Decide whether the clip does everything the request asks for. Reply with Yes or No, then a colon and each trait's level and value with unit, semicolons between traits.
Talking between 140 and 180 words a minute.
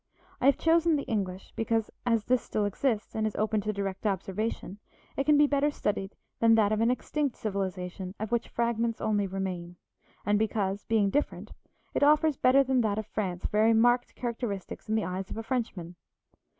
No: average, 190 wpm